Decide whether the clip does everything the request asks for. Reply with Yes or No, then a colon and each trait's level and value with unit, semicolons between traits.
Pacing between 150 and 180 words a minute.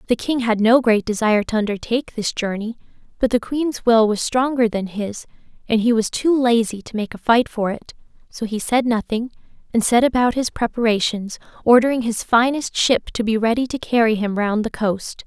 No: average, 200 wpm